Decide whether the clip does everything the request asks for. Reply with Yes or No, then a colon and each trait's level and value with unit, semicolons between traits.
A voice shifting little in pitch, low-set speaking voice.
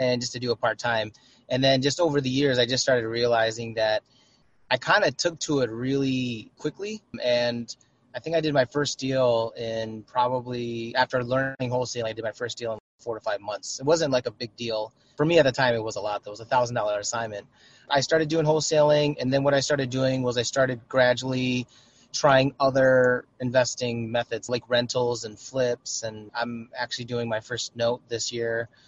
Yes: narrow, 2.2 semitones; low, 125 Hz